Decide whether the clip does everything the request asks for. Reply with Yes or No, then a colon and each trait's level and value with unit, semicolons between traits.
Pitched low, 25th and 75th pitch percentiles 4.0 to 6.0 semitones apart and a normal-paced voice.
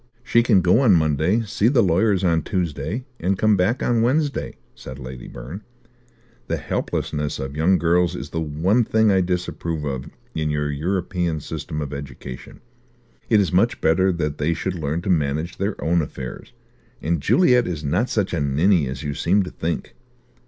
Yes: very low, 85 Hz; average, 4.7 semitones; average, 180 wpm